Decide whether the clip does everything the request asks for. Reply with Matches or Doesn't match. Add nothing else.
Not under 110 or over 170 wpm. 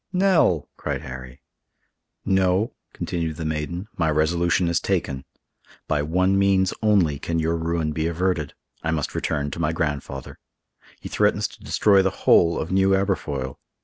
Matches